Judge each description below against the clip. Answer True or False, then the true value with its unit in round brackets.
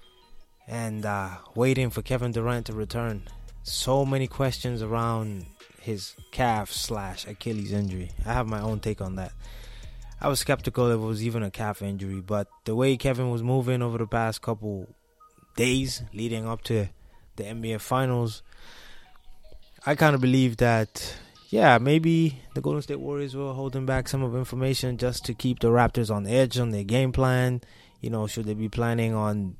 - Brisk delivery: False (175 wpm)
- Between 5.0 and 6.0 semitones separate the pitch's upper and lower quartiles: False (3.1 semitones)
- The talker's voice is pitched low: True (115 Hz)